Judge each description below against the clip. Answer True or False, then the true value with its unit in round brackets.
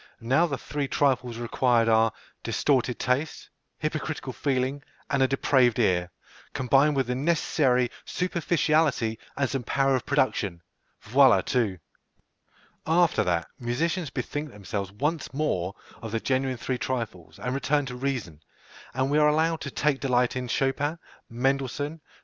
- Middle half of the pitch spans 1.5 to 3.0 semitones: False (3.5 semitones)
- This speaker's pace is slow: False (145 wpm)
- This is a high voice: False (130 Hz)